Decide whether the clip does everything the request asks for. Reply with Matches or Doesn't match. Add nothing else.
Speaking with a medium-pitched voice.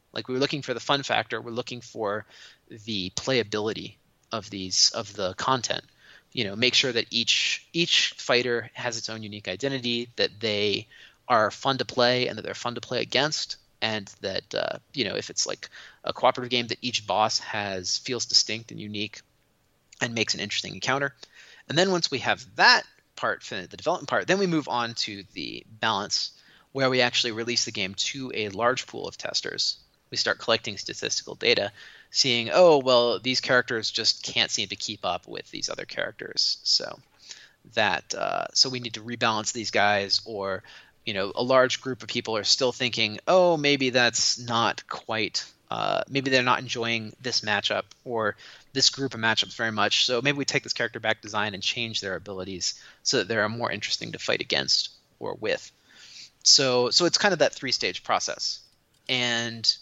Doesn't match